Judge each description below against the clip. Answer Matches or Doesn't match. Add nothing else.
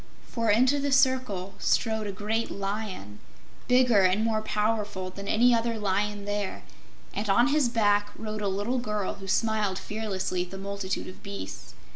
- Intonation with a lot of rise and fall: Doesn't match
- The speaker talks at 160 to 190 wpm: Matches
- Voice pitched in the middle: Doesn't match